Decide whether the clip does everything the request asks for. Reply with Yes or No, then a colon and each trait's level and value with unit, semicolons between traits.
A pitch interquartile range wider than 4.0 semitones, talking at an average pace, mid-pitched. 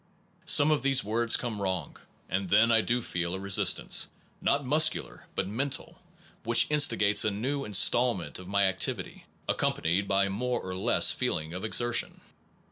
No: average, 4.5 semitones; average, 155 wpm; low, 110 Hz